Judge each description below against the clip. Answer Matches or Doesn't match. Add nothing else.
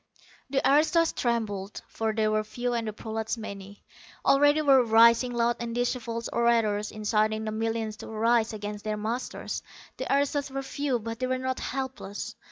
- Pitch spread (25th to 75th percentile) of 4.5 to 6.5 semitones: Doesn't match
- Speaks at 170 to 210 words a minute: Matches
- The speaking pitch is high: Matches